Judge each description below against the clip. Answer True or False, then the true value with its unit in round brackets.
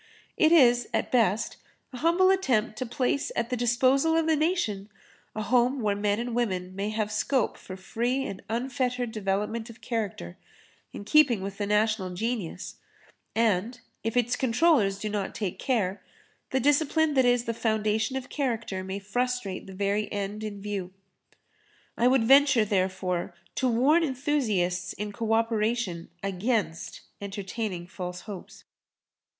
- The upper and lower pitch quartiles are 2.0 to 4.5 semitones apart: True (4.0 semitones)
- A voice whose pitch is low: False (225 Hz)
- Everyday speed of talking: True (150 wpm)